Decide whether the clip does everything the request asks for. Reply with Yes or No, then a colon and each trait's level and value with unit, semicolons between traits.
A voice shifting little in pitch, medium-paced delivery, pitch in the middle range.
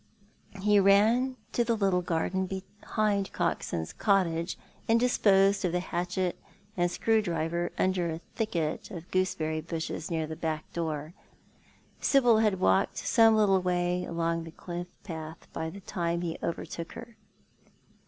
No: average, 3.3 semitones; average, 145 wpm; medium, 180 Hz